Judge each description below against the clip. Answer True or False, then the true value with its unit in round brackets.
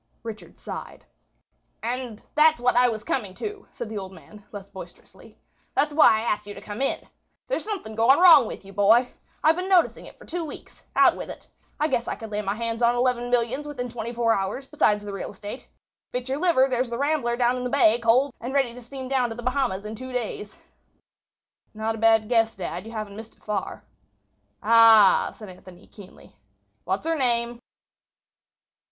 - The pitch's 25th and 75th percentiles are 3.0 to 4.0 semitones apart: True (3.5 semitones)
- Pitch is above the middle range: True (235 Hz)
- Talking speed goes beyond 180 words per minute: True (205 wpm)